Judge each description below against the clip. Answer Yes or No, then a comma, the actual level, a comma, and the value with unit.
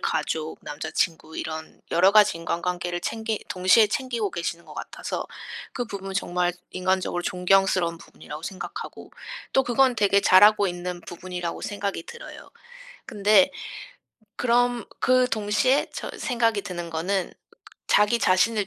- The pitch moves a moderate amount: Yes, average, 3.6 semitones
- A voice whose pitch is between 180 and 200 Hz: Yes, high, 190 Hz